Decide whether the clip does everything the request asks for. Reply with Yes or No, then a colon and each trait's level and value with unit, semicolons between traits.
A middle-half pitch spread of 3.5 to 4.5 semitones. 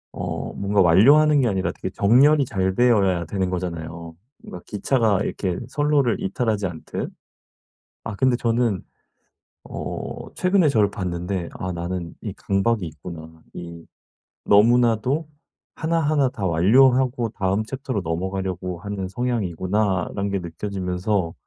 No: average, 5.2 semitones